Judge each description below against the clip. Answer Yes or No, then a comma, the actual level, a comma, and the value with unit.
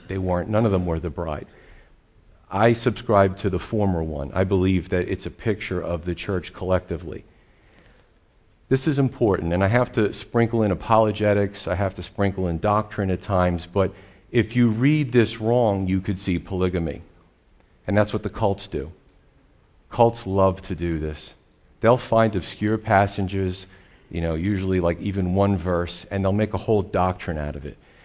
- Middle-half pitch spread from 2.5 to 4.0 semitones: Yes, average, 3.2 semitones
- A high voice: No, very low, 95 Hz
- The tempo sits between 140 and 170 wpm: No, average, 180 wpm